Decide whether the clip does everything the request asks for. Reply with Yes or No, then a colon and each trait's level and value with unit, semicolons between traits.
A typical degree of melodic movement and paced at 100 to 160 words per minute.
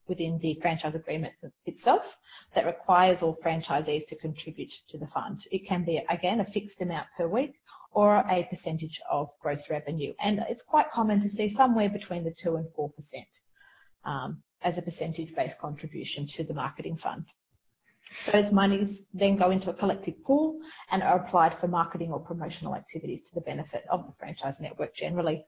No: average, 4.0 semitones; average, 175 wpm